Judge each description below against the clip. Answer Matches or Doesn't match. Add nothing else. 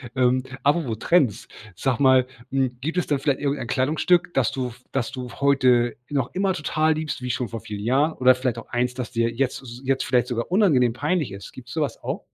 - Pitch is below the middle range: Matches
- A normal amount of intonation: Matches